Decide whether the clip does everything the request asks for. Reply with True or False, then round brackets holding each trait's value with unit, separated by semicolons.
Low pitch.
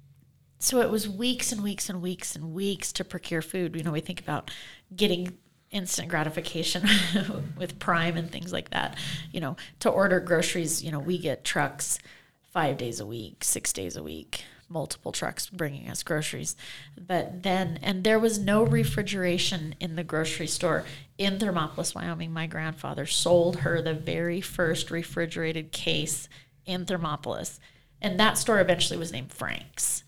False (170 Hz)